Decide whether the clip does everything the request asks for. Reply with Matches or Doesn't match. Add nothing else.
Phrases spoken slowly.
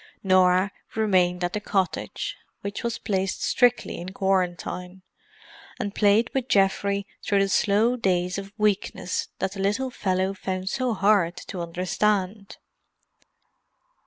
Matches